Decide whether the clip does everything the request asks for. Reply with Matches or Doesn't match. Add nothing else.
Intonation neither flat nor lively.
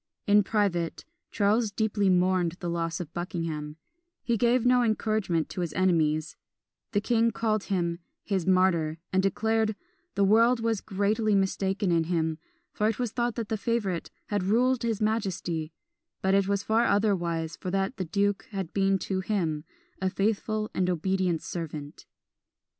Matches